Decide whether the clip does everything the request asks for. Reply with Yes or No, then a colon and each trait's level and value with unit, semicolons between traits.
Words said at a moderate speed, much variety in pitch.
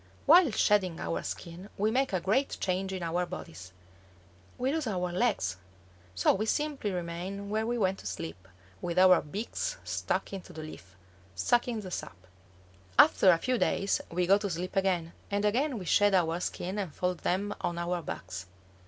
No: average, 180 wpm; average, 3.7 semitones